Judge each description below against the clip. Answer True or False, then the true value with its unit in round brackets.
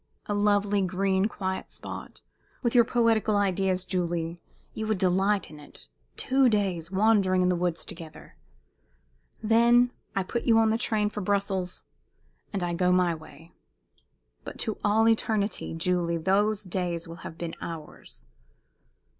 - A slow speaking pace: False (145 wpm)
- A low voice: False (190 Hz)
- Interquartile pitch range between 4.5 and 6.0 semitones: False (3.3 semitones)